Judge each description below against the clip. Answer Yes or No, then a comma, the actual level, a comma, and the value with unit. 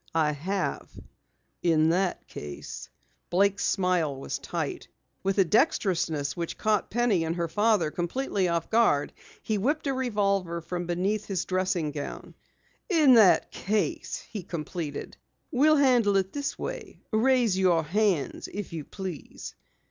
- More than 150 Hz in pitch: Yes, high, 190 Hz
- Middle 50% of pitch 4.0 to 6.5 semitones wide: Yes, average, 4.4 semitones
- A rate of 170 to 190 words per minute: No, average, 140 wpm